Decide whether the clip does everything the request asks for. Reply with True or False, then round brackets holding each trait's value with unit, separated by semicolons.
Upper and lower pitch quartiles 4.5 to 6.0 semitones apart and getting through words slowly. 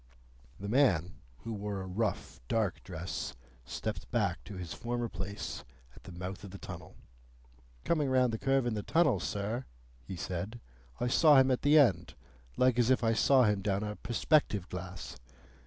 False (4.8 semitones; 175 wpm)